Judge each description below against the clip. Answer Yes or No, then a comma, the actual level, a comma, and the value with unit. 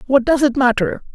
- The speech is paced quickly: Yes, fast, 210 wpm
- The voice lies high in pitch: Yes, very high, 255 Hz